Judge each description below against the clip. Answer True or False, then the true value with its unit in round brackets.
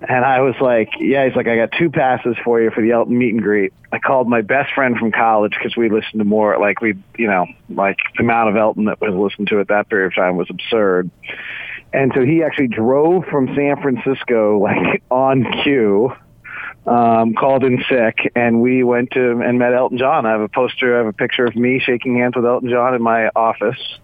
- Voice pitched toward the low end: True (120 Hz)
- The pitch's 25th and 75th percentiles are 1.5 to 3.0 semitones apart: True (2.4 semitones)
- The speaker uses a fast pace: True (230 wpm)